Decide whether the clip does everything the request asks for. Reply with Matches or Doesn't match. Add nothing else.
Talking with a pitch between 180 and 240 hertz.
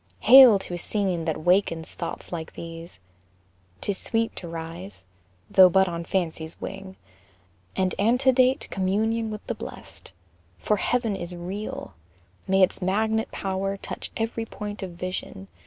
Matches